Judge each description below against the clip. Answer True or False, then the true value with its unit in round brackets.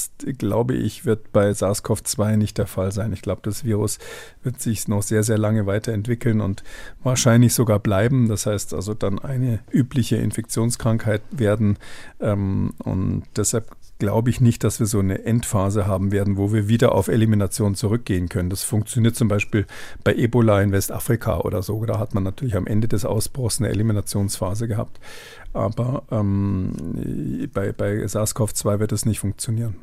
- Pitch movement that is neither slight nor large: False (2.1 semitones)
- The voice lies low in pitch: True (105 Hz)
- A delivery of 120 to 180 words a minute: True (165 wpm)